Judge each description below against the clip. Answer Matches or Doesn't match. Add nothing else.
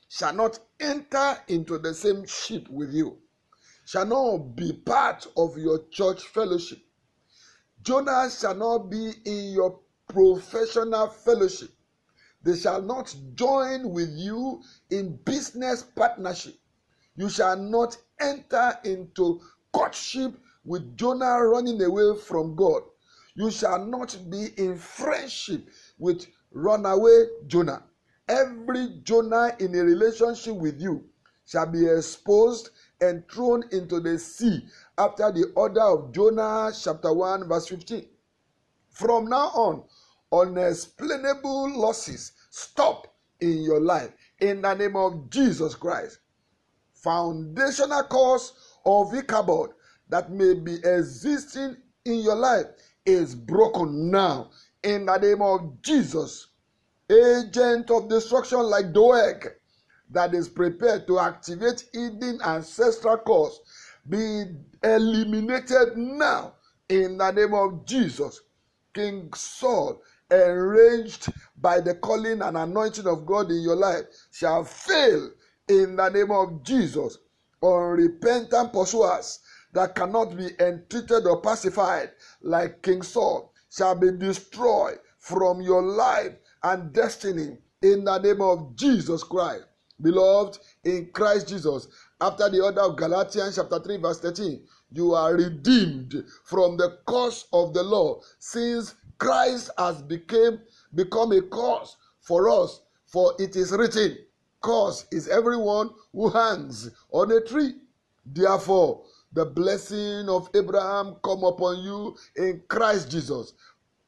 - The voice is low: Doesn't match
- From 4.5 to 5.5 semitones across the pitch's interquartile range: Matches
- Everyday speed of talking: Doesn't match